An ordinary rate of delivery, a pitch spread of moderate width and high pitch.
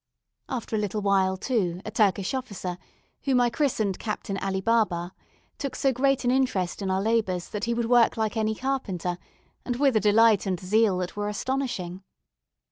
Yes: average, 180 wpm; average, 4.3 semitones; high, 215 Hz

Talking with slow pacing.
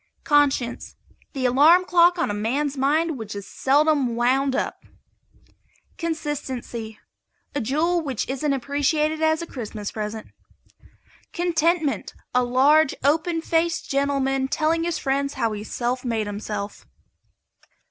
Yes: slow, 125 wpm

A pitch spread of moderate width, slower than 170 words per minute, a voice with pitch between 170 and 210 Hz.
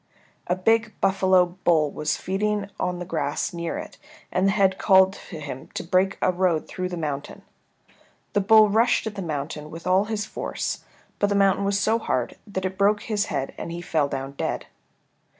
No: average, 3.3 semitones; average, 195 wpm; medium, 185 Hz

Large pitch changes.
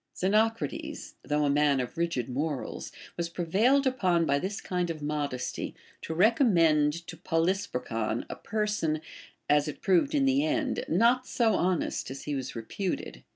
Yes: wide, 6.3 semitones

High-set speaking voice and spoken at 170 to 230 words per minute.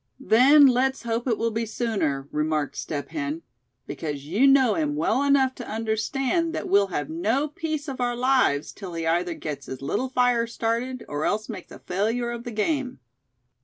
Yes: high, 230 Hz; average, 185 wpm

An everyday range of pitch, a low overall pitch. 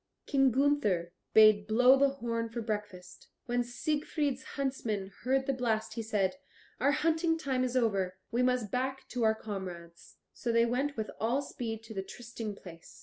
No: average, 3.8 semitones; high, 235 Hz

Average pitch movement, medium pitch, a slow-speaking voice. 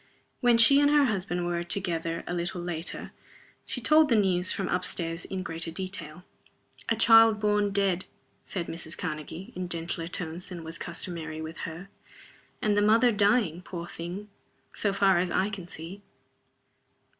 No: average, 3.5 semitones; medium, 180 Hz; average, 165 wpm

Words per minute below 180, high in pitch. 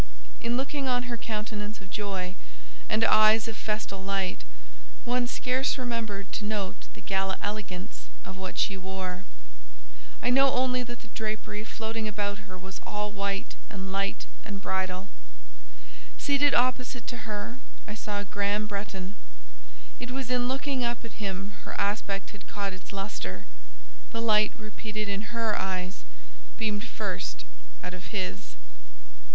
Yes: average, 145 wpm; high, 210 Hz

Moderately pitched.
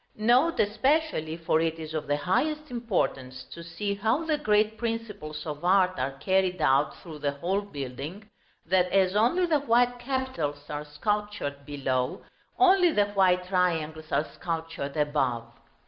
Yes: medium, 180 Hz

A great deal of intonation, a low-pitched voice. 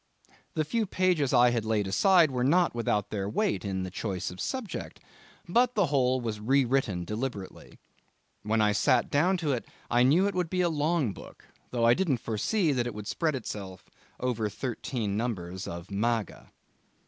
Yes: wide, 7.1 semitones; low, 125 Hz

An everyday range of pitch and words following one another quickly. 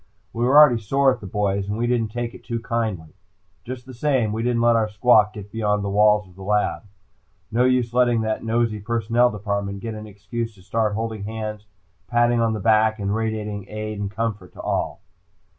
No: narrow, 2.2 semitones; fast, 210 wpm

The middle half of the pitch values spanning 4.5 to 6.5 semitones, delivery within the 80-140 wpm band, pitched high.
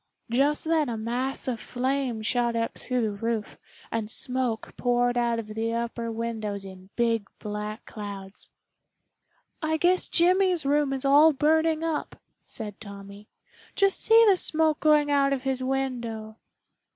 No: average, 4.9 semitones; average, 150 wpm; high, 245 Hz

